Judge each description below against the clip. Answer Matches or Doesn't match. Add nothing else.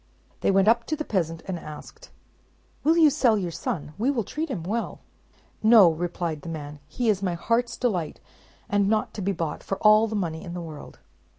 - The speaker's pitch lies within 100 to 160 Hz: Doesn't match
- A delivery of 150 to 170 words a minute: Doesn't match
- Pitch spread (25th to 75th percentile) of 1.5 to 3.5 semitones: Doesn't match